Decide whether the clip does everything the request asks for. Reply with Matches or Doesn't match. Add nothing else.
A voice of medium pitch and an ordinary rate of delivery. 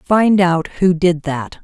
Matches